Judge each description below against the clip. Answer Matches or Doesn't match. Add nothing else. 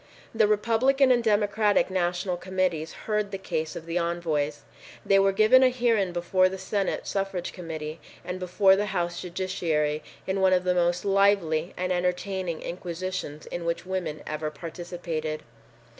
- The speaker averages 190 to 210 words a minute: Doesn't match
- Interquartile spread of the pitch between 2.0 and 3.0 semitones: Matches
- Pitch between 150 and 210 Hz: Matches